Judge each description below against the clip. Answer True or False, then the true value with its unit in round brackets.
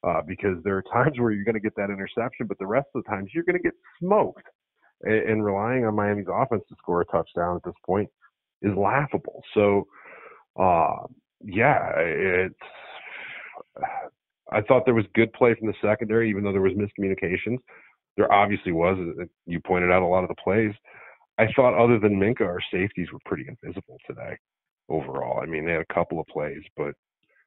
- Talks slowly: False (190 wpm)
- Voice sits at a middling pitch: False (105 Hz)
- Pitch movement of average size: True (3.2 semitones)